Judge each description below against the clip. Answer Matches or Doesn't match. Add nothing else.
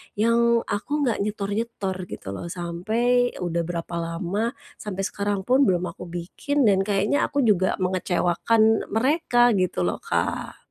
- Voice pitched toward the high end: Matches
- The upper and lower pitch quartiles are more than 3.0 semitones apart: Matches